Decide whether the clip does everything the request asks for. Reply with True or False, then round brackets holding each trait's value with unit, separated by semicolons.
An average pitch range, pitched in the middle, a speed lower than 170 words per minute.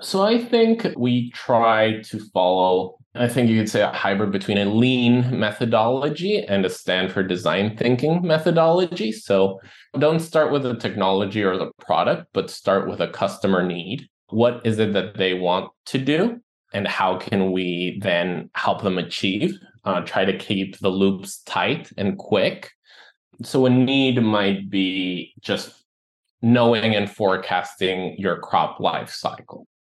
False (4.9 semitones; 110 Hz; 155 wpm)